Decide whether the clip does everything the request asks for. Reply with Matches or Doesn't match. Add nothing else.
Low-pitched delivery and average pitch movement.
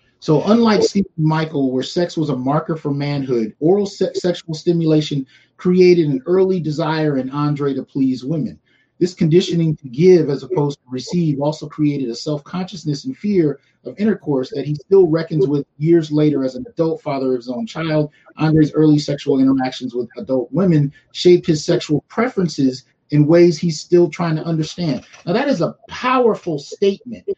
Doesn't match